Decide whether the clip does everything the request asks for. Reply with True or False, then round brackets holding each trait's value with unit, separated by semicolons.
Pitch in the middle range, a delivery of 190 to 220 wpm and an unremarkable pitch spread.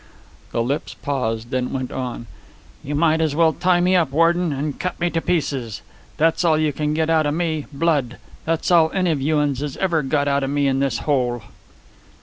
True (150 Hz; 200 wpm; 3.4 semitones)